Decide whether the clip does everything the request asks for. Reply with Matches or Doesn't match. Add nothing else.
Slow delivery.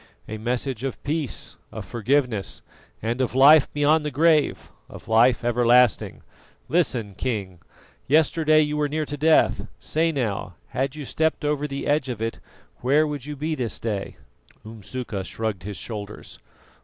Doesn't match